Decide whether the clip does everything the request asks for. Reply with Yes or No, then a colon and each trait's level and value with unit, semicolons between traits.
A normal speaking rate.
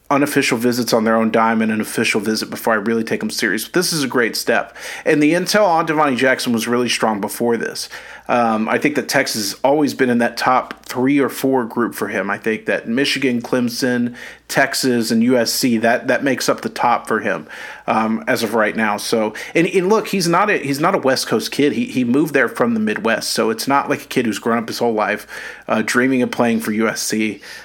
No: fast, 230 wpm